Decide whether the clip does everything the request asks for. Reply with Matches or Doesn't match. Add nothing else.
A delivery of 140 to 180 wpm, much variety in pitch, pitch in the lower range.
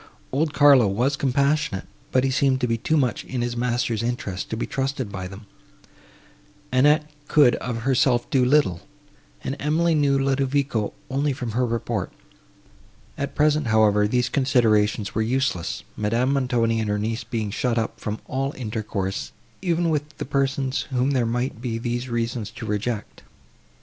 Doesn't match